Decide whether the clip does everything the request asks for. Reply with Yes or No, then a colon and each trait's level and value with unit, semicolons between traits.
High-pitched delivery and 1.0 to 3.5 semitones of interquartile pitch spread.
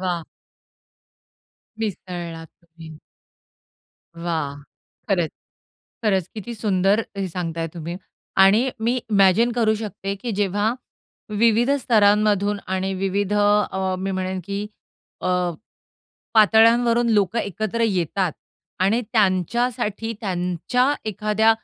Yes: high, 200 Hz; average, 3.2 semitones